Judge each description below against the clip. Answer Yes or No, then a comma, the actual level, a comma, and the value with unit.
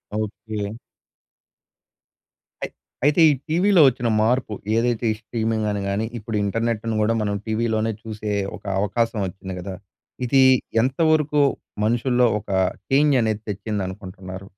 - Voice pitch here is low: Yes, low, 110 Hz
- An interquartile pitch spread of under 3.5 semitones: Yes, average, 2.8 semitones